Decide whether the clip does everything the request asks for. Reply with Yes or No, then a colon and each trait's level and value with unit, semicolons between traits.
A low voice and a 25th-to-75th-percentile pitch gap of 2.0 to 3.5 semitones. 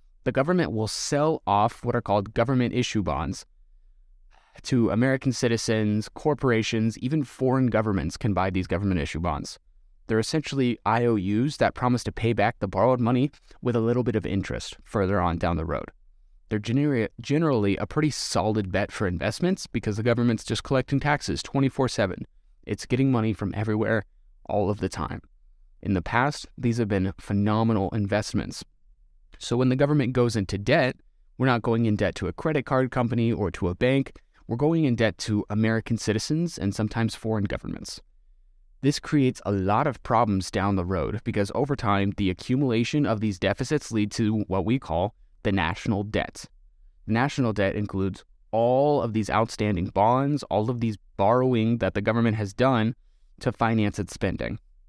No: low, 110 Hz; average, 4.1 semitones